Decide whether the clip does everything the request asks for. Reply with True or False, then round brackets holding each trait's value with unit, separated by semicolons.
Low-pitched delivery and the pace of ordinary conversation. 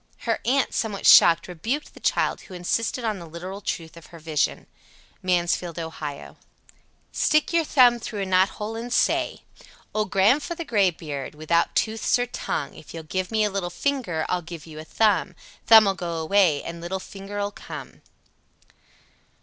False (190 Hz; 165 wpm)